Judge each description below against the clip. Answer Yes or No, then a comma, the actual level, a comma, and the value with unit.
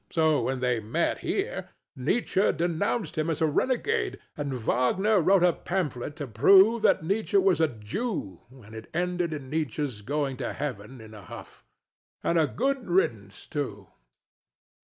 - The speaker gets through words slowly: No, average, 160 wpm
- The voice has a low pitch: No, medium, 155 Hz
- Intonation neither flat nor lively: No, wide, 7.3 semitones